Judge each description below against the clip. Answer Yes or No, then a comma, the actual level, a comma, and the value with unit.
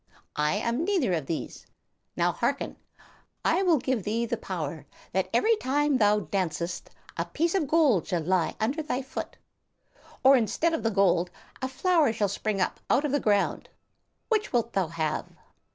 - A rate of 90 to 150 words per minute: No, average, 170 wpm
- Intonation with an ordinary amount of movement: No, wide, 7.3 semitones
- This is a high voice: Yes, high, 235 Hz